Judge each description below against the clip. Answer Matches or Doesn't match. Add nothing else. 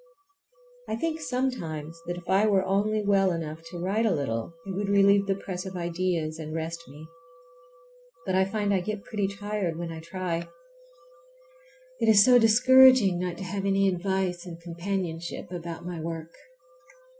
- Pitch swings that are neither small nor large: Matches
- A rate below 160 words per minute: Doesn't match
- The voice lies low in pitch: Doesn't match